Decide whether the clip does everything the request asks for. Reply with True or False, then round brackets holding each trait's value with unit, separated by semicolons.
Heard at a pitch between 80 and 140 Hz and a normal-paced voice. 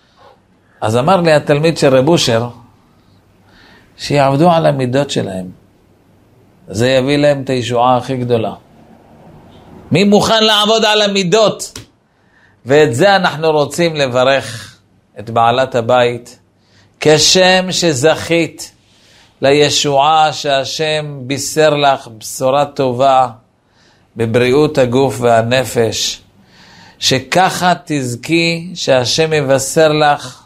False (135 Hz; 95 wpm)